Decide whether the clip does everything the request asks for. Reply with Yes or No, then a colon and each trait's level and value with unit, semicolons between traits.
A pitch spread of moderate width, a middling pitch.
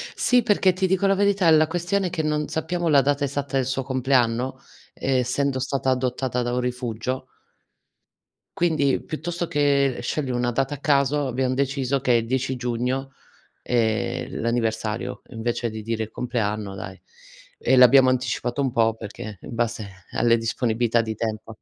No: average, 3.3 semitones; low, 130 Hz